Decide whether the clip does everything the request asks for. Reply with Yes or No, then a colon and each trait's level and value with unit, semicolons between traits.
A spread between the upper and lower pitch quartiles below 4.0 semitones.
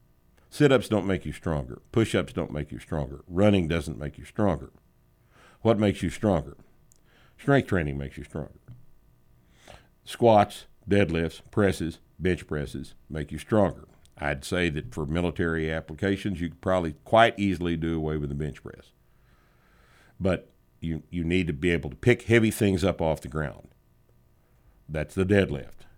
No: average, 4.7 semitones